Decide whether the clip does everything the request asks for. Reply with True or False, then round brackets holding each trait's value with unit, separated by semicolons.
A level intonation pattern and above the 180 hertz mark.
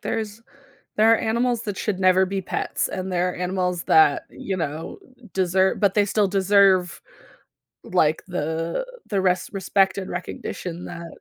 True (2.1 semitones; 190 Hz)